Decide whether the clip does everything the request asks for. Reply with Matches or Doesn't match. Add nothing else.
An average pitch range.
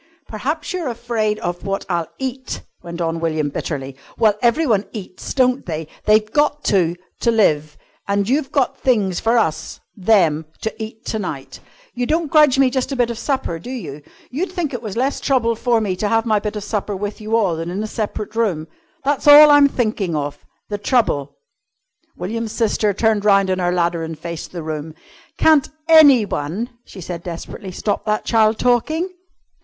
Doesn't match